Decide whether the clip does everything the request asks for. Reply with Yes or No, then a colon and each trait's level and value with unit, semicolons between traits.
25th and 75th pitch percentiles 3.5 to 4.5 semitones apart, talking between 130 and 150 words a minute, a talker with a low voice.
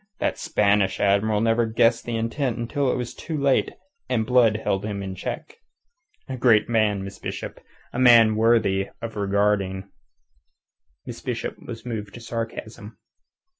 No: narrow, 2.6 semitones; average, 145 wpm; low, 115 Hz